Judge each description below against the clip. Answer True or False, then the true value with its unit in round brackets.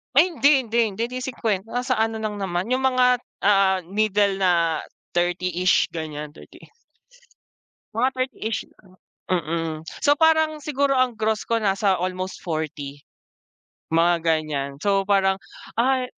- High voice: True (200 Hz)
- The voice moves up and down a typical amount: False (6.2 semitones)